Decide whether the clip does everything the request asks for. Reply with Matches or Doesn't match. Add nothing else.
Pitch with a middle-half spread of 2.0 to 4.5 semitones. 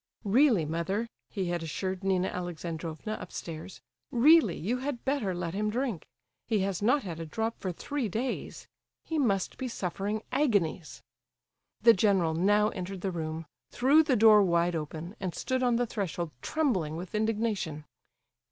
Doesn't match